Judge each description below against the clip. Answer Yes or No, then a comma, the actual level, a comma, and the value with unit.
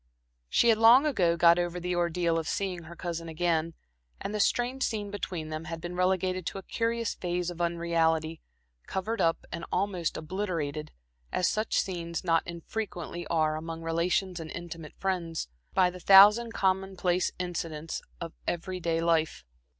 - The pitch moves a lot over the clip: No, narrow, 2.5 semitones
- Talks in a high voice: No, medium, 175 Hz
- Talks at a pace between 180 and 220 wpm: No, average, 160 wpm